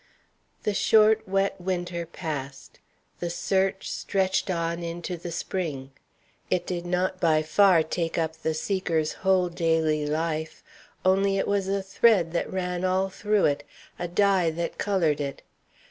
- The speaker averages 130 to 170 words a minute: Yes, average, 145 wpm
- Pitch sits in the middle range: Yes, medium, 175 Hz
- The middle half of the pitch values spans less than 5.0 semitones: Yes, average, 2.9 semitones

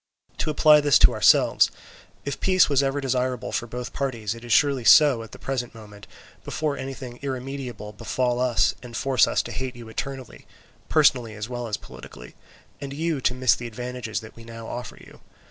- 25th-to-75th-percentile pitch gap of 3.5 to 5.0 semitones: No, average, 2.9 semitones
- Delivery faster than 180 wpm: Yes, average, 190 wpm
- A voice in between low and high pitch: No, low, 125 Hz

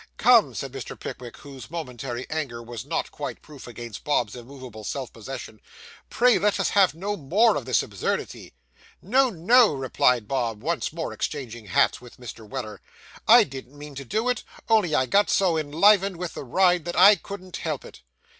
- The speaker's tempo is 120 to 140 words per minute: No, average, 180 wpm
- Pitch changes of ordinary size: No, wide, 7.7 semitones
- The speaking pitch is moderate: Yes, medium, 145 Hz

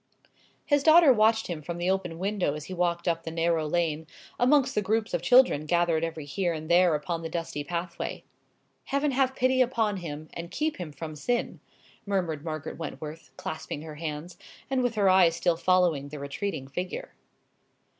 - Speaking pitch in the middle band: Yes, medium, 175 Hz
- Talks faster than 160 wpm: Yes, average, 180 wpm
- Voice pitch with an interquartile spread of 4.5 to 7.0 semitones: Yes, average, 5.0 semitones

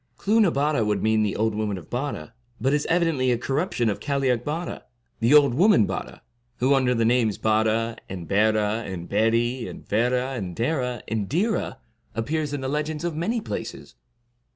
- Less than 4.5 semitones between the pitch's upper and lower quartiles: No, average, 5.2 semitones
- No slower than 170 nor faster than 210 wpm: Yes, average, 180 wpm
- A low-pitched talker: Yes, low, 125 Hz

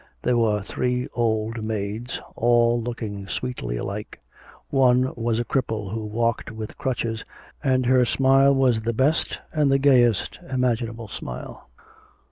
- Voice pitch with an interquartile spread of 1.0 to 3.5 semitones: Yes, narrow, 2.6 semitones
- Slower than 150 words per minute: Yes, slow, 135 wpm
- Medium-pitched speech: No, low, 120 Hz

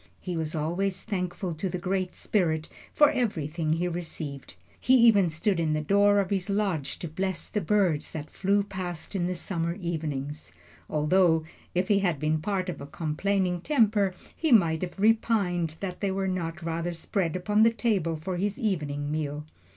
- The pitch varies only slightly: No, average, 3.7 semitones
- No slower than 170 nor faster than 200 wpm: Yes, average, 175 wpm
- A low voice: No, medium, 180 Hz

